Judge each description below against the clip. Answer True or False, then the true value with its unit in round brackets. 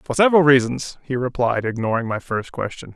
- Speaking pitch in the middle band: False (130 Hz)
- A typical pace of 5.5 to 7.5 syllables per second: True (5.7 syllables/s)